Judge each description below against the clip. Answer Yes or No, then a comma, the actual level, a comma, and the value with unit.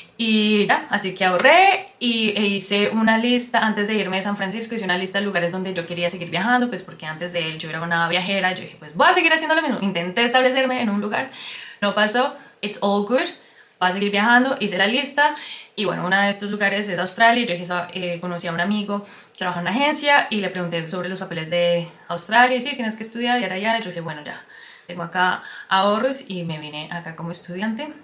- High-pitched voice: Yes, high, 200 Hz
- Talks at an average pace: No, fast, 235 wpm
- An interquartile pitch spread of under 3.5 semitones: No, average, 4.9 semitones